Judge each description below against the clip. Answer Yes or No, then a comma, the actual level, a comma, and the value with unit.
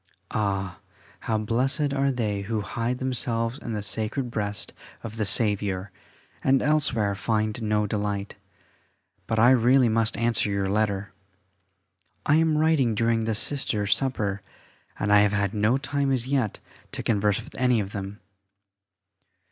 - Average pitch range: Yes, average, 3.6 semitones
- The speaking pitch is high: No, low, 110 Hz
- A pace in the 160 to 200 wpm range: No, average, 150 wpm